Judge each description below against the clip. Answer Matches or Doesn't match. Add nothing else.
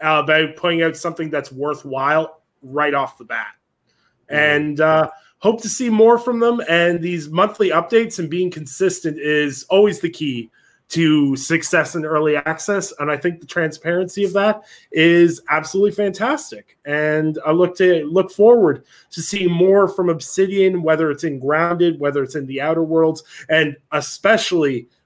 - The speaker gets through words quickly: Doesn't match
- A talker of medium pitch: Matches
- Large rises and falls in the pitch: Doesn't match